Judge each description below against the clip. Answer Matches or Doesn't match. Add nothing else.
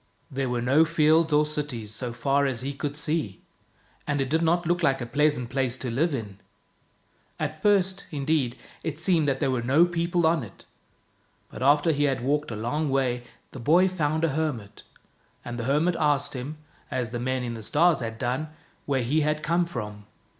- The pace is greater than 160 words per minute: Matches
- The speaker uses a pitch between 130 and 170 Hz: Matches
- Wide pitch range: Doesn't match